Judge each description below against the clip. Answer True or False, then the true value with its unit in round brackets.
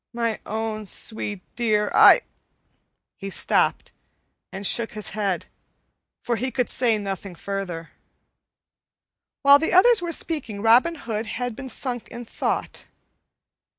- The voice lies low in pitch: False (225 Hz)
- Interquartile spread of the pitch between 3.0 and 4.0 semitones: True (3.5 semitones)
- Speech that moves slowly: True (130 wpm)